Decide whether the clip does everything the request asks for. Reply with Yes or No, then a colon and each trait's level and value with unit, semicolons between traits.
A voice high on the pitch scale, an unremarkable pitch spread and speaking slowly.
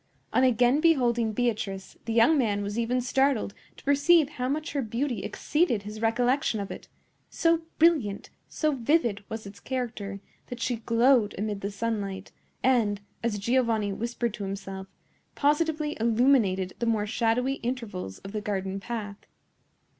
No: high, 230 Hz; average, 4.2 semitones; average, 150 wpm